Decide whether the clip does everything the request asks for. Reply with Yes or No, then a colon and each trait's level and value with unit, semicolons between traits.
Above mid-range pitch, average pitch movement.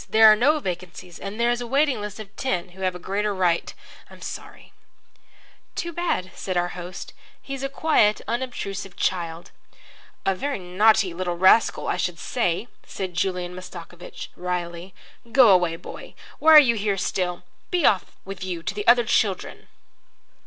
Yes: high, 195 Hz; average, 4.5 semitones